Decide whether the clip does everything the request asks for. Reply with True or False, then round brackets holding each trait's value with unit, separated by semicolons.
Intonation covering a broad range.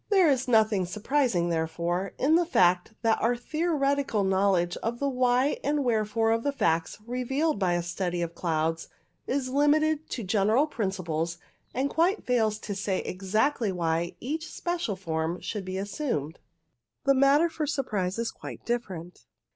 True (7.4 semitones)